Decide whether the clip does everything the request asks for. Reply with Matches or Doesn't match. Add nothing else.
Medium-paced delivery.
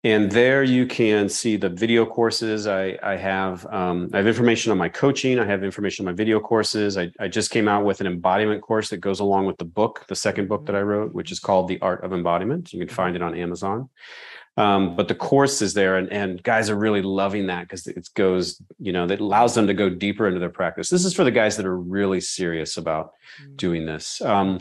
Doesn't match